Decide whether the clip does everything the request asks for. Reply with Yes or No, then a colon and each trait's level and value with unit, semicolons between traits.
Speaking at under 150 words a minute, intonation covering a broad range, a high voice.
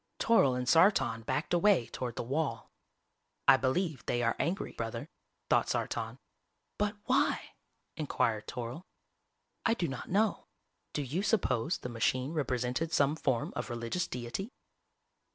No: slow, 135 wpm; wide, 6.4 semitones; low, 135 Hz